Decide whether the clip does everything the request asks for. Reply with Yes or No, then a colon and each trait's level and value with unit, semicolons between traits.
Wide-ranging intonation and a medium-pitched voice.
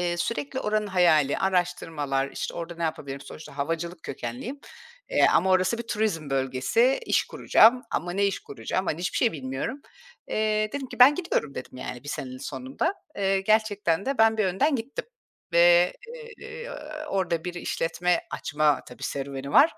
Yes: wide, 6.8 semitones; medium, 180 Hz